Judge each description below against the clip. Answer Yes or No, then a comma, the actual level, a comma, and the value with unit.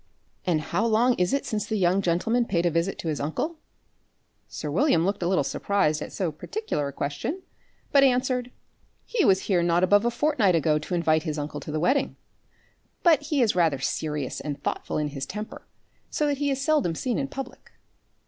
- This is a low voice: No, high, 190 Hz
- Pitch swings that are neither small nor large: No, wide, 8.3 semitones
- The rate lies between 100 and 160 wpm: No, average, 200 wpm